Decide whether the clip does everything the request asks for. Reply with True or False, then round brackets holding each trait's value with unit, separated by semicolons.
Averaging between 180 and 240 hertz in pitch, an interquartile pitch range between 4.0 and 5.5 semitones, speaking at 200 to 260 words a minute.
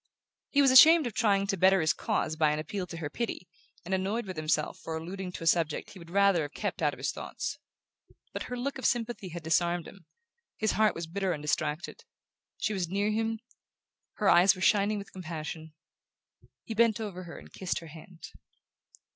True (185 Hz; 4.3 semitones; 205 wpm)